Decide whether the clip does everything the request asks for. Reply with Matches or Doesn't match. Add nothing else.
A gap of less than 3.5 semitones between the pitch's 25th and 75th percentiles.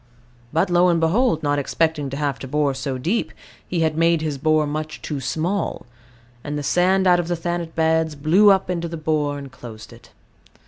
Matches